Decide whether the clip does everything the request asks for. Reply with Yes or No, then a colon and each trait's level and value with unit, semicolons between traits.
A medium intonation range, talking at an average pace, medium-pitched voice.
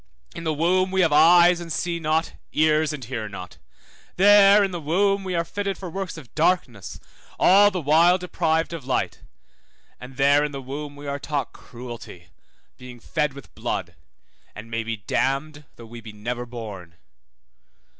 No: wide, 5.9 semitones; average, 175 wpm; medium, 150 Hz